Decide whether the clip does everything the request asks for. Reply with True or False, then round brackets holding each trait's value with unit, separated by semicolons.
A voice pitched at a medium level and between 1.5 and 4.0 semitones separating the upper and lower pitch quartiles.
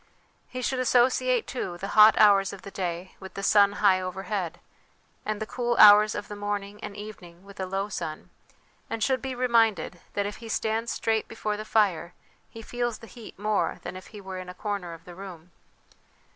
False (205 Hz; 2.9 semitones)